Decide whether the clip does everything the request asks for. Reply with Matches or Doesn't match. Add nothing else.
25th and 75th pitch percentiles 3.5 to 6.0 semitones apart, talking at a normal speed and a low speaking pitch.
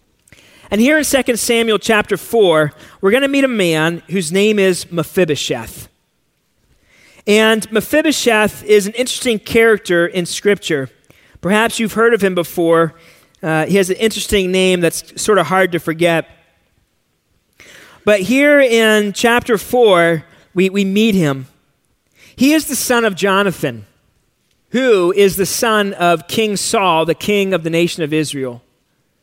Doesn't match